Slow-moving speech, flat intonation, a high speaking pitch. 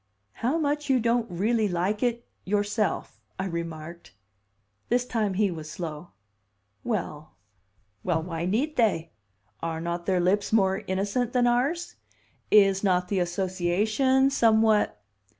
No: slow, 130 wpm; average, 5.2 semitones; high, 200 Hz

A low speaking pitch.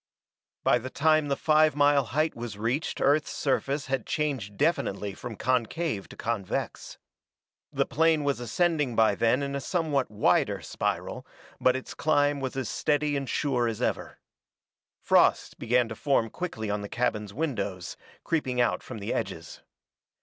Yes: low, 130 Hz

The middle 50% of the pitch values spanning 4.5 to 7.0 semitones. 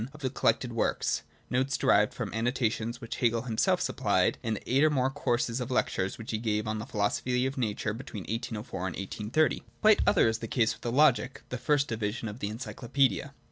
No: average, 3.1 semitones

